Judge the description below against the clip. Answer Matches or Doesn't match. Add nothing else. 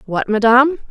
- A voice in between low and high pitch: Doesn't match